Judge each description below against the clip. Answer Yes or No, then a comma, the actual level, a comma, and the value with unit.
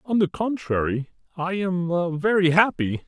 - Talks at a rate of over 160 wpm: No, slow, 135 wpm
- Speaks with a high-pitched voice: No, medium, 175 Hz